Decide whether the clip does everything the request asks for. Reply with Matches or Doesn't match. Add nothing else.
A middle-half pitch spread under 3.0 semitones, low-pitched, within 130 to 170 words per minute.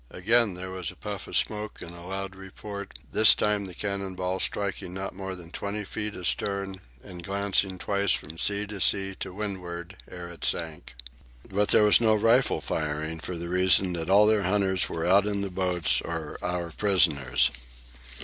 Doesn't match